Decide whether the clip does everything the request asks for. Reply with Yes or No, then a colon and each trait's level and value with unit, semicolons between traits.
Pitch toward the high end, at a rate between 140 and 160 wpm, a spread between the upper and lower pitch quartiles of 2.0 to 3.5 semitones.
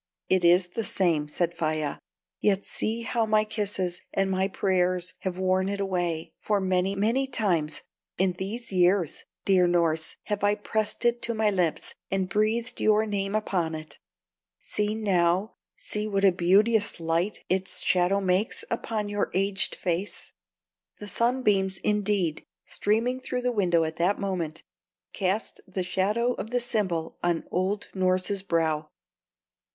Yes: high, 195 Hz; average, 150 wpm; average, 3.0 semitones